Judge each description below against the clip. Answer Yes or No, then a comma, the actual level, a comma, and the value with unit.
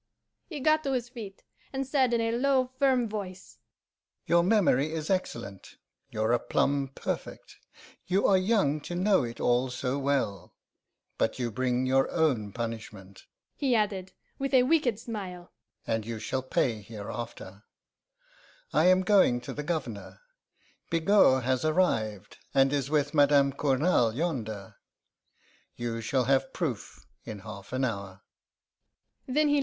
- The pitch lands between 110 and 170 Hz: Yes, medium, 140 Hz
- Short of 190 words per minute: Yes, average, 140 wpm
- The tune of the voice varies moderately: No, wide, 8.9 semitones